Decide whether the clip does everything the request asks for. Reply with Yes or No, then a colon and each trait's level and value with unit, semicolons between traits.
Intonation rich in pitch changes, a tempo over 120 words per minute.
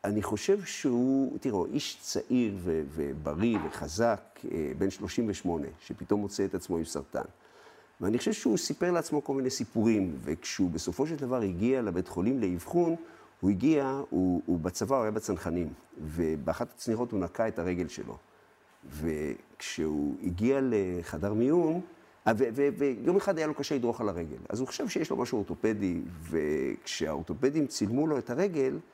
Yes: wide, 7.5 semitones; average, 145 wpm